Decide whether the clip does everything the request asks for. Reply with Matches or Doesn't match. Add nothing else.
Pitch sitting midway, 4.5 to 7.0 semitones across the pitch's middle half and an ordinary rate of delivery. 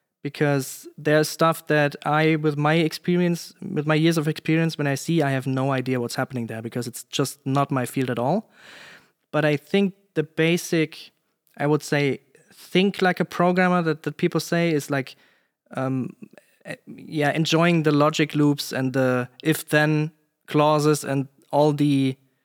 Doesn't match